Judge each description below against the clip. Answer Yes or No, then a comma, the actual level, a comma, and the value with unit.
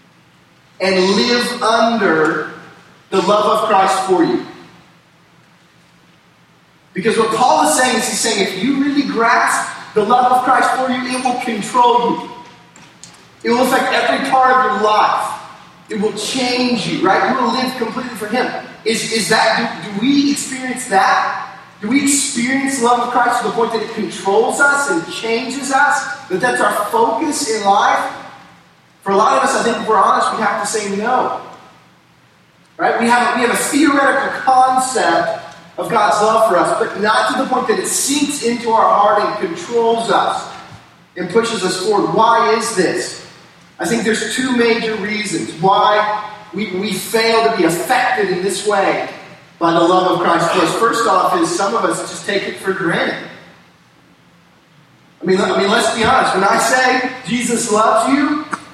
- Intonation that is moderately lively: Yes, average, 4.6 semitones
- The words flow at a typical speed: Yes, average, 180 wpm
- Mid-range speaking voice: No, high, 225 Hz